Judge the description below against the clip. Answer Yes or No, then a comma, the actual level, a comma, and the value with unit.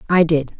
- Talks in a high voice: No, medium, 165 Hz